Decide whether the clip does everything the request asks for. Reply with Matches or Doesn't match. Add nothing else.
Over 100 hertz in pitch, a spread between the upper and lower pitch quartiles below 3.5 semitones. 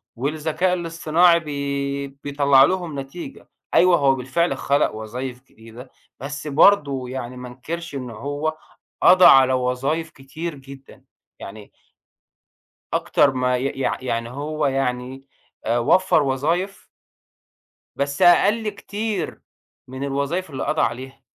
Doesn't match